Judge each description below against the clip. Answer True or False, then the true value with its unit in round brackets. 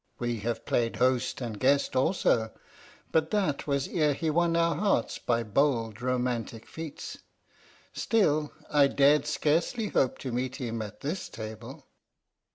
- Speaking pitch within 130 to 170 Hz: True (135 Hz)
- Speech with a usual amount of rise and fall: True (4.5 semitones)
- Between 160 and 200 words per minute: False (145 wpm)